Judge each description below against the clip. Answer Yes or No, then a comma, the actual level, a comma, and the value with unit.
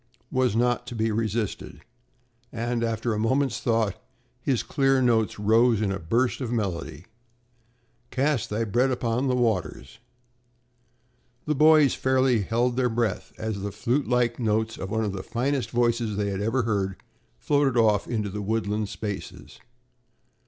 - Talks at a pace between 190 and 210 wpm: No, average, 150 wpm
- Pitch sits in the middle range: No, low, 115 Hz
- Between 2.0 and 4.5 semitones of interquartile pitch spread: Yes, average, 3.0 semitones